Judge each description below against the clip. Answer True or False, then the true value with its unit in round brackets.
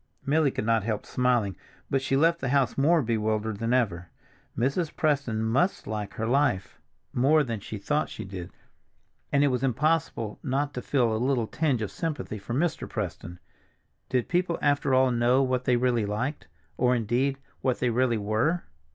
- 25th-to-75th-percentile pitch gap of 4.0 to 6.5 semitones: True (4.3 semitones)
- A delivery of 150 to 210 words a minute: True (175 wpm)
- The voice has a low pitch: True (125 Hz)